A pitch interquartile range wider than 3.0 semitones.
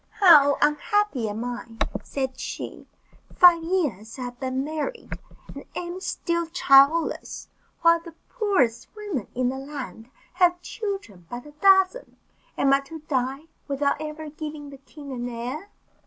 Yes: average, 5.0 semitones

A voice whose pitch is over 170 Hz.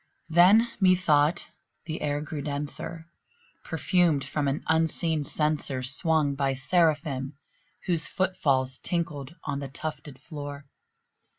No: medium, 150 Hz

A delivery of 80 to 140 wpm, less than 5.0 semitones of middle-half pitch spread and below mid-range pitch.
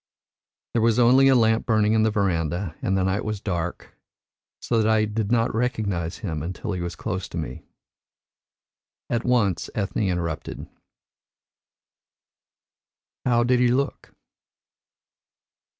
Yes: slow, 135 wpm; average, 4.5 semitones; low, 105 Hz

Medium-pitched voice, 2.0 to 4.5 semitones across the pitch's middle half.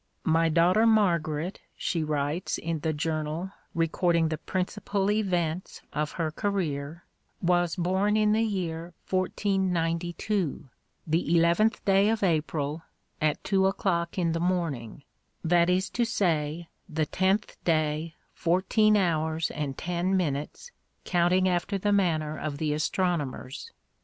Yes: medium, 170 Hz; average, 3.3 semitones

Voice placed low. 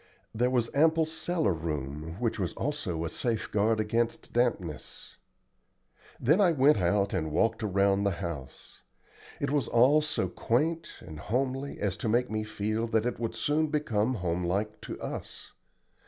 Yes: low, 110 Hz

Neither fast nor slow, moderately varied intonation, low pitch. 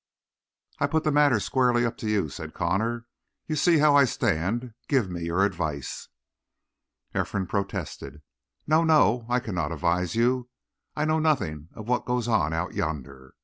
No: average, 160 wpm; wide, 7.2 semitones; low, 110 Hz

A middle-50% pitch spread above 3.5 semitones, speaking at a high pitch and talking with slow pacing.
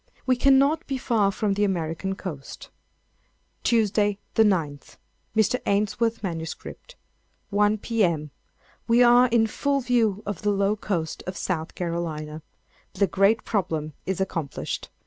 Yes: average, 5.0 semitones; high, 200 Hz; slow, 130 wpm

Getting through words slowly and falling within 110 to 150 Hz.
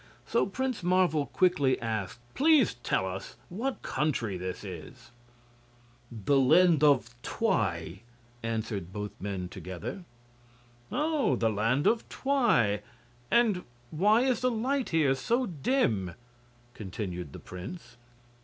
Yes: slow, 115 wpm; low, 135 Hz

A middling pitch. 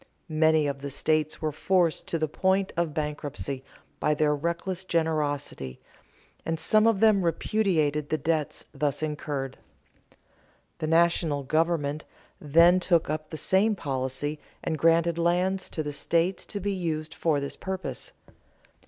Yes: medium, 160 Hz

